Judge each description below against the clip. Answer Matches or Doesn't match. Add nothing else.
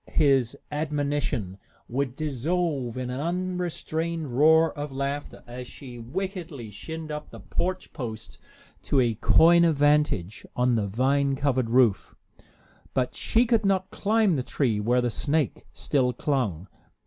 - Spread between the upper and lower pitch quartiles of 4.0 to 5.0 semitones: Matches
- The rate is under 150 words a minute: Matches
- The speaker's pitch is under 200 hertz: Matches